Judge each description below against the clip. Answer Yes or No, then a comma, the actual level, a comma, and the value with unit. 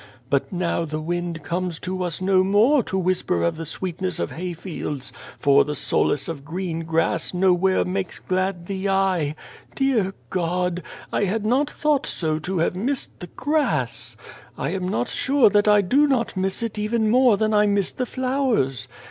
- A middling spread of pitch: Yes, average, 4.0 semitones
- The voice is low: No, medium, 185 Hz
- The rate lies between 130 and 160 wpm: No, average, 175 wpm